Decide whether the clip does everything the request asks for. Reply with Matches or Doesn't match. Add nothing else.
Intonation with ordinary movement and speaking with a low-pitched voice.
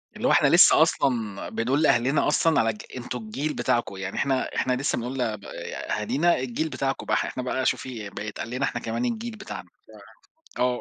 Matches